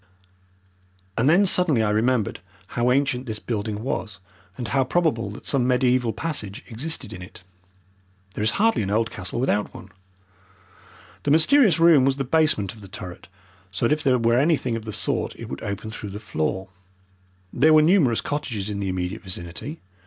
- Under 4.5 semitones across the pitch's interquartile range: No, wide, 5.6 semitones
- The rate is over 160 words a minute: Yes, average, 180 wpm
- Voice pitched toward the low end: Yes, low, 120 Hz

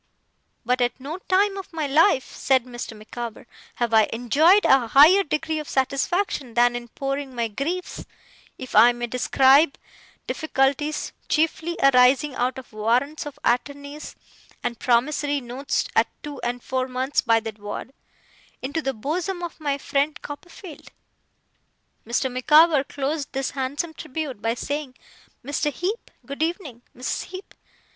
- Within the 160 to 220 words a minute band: No, average, 145 wpm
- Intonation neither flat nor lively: Yes, average, 3.9 semitones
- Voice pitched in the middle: No, very high, 275 Hz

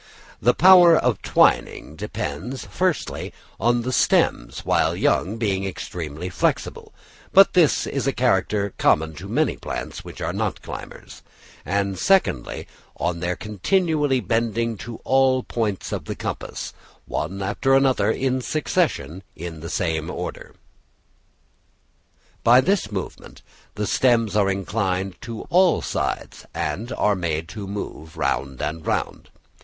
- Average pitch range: No, wide, 6.3 semitones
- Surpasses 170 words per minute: No, slow, 135 wpm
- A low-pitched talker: Yes, low, 105 Hz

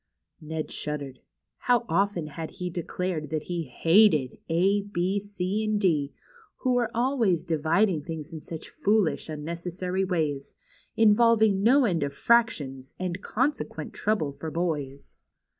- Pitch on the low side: No, medium, 175 Hz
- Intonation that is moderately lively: Yes, average, 4.9 semitones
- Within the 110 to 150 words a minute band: Yes, average, 140 wpm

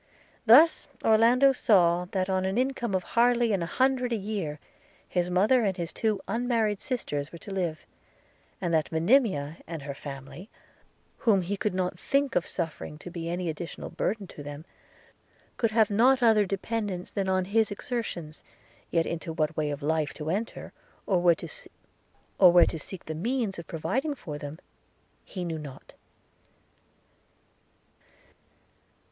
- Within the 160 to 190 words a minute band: No, average, 150 wpm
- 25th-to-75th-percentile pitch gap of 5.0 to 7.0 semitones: Yes, wide, 5.5 semitones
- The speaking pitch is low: No, medium, 185 Hz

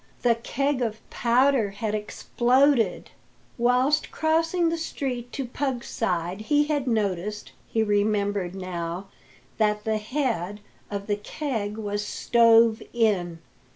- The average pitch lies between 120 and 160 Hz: No, high, 225 Hz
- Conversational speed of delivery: No, slow, 120 wpm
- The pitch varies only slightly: No, average, 4.0 semitones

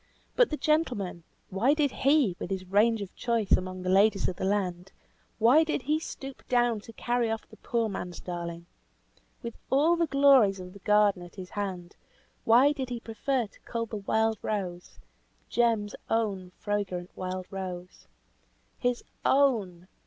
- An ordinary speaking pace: Yes, average, 165 wpm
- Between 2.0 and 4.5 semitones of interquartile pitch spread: No, average, 4.9 semitones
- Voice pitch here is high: Yes, high, 210 Hz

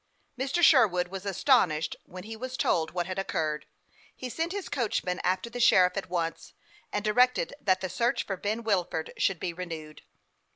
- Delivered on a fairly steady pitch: No, average, 5.1 semitones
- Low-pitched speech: No, high, 195 Hz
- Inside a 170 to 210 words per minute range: Yes, average, 175 wpm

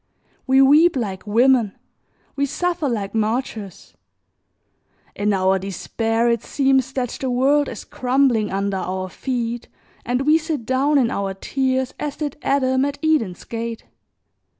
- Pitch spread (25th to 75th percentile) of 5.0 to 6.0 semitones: No, average, 4.4 semitones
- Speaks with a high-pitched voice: Yes, very high, 250 Hz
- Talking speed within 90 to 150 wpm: Yes, average, 140 wpm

